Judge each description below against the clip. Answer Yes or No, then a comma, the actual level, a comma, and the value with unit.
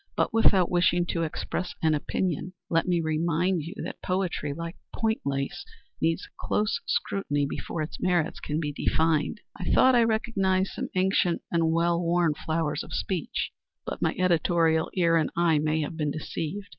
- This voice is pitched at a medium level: Yes, medium, 170 Hz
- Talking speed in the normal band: Yes, average, 170 wpm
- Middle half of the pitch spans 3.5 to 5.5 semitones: No, average, 2.7 semitones